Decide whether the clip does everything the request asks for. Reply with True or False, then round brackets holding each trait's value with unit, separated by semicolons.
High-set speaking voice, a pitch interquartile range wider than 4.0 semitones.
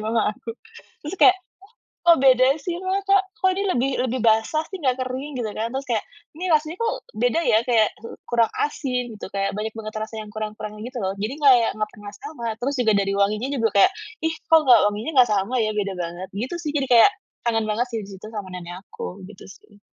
True (230 Hz; 4.4 semitones)